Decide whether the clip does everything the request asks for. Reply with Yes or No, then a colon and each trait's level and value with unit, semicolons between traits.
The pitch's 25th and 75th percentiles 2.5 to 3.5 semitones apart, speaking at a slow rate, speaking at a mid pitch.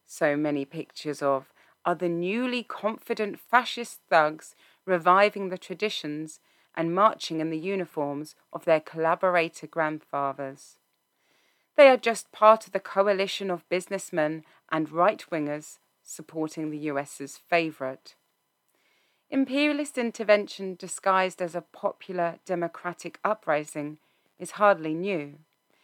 No: average, 4.2 semitones; slow, 115 wpm; medium, 175 Hz